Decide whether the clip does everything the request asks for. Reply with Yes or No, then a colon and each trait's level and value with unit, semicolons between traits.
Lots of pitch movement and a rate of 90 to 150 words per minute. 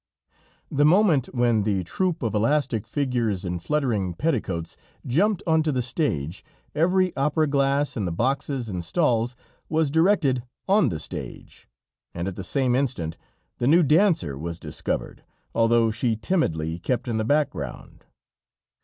Yes: wide, 7.3 semitones; average, 145 wpm